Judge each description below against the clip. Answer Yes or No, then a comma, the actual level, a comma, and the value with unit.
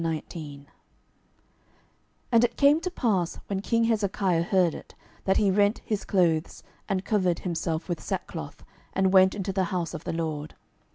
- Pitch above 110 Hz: Yes, medium, 185 Hz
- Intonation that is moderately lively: Yes, average, 3.6 semitones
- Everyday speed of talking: Yes, average, 160 wpm